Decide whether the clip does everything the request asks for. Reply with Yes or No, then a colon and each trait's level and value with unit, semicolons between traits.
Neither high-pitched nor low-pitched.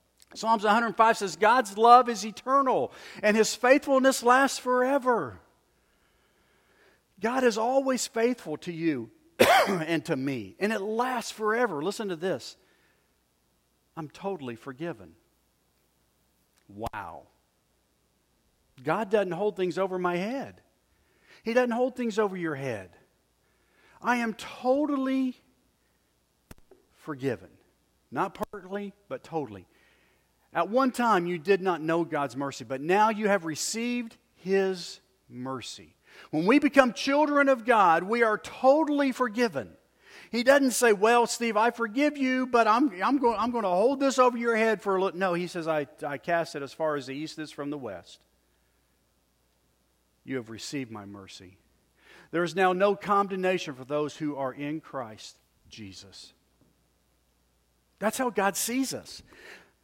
No: high, 195 Hz